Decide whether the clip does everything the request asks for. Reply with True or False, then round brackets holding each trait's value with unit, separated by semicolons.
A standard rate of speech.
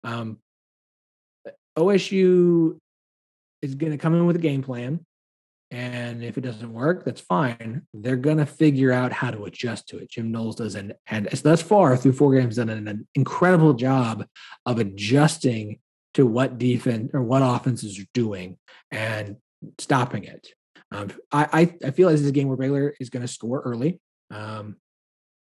True (175 wpm)